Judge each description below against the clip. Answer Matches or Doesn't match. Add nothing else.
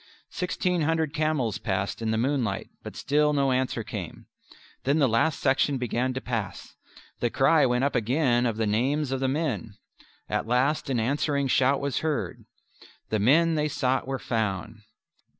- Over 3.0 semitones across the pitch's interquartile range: Matches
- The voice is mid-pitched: Doesn't match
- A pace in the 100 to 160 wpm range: Doesn't match